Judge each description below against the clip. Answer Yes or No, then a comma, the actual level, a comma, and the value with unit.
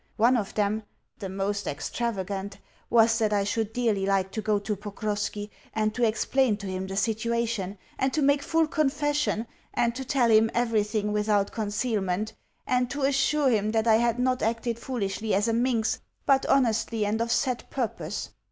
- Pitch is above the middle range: Yes, high, 220 Hz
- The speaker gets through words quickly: No, average, 175 wpm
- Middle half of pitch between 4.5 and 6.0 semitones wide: No, average, 3.0 semitones